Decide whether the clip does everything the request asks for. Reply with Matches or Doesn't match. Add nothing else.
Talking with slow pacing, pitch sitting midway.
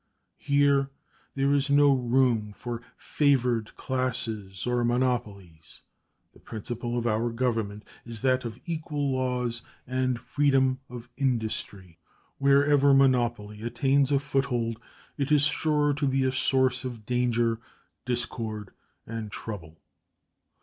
Doesn't match